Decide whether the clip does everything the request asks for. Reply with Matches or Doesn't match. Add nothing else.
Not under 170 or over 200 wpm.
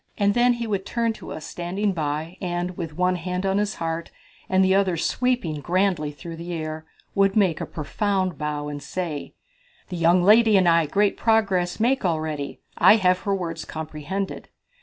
Matches